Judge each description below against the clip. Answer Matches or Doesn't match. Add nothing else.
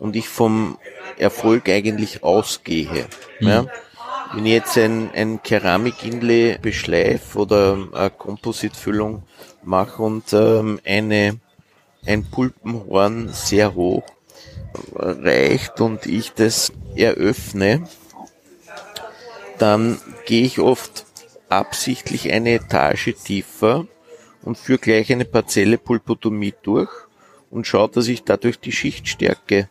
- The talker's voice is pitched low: Matches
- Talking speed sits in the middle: Doesn't match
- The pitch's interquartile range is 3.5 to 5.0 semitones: Doesn't match